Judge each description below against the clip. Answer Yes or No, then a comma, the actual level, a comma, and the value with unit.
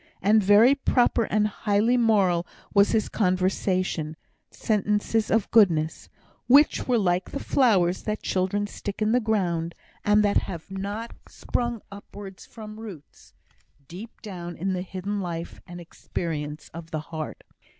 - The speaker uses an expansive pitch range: No, average, 3.6 semitones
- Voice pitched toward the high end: Yes, high, 200 Hz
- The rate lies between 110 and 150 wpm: Yes, average, 145 wpm